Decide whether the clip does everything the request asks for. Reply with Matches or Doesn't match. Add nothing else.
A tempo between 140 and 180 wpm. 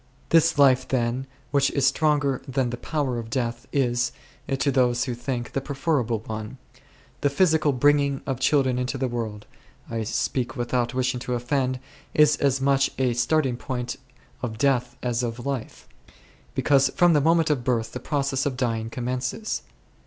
Matches